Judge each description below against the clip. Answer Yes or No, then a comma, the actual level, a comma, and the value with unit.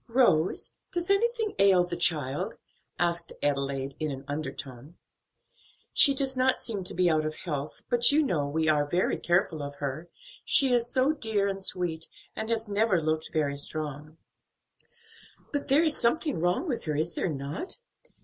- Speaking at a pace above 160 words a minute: Yes, average, 170 wpm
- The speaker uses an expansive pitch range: Yes, wide, 7.9 semitones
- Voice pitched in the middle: Yes, medium, 175 Hz